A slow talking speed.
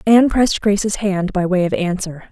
No: fast, 205 wpm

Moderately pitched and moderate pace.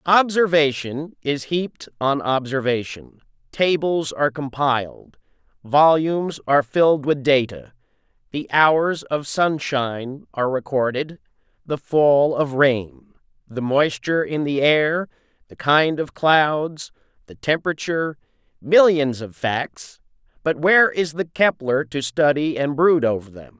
No: medium, 145 Hz; slow, 120 wpm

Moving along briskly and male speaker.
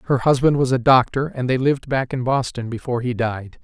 Yes: fast, 230 wpm; male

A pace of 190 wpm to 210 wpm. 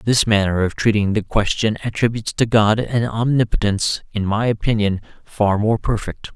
No: average, 160 wpm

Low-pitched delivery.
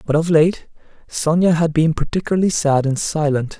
No: medium, 160 Hz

